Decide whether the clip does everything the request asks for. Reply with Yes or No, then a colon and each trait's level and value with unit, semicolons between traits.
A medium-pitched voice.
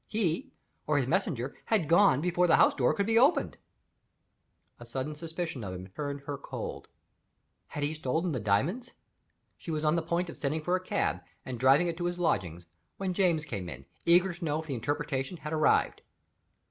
Yes: medium, 155 Hz